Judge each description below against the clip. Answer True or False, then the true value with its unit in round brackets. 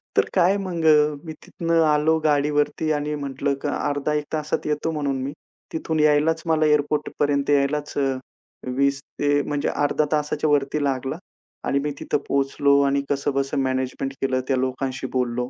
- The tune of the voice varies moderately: False (1.7 semitones)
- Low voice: False (145 Hz)